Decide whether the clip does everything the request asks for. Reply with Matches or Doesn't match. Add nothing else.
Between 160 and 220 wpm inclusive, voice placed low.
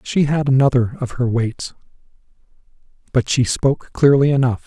Doesn't match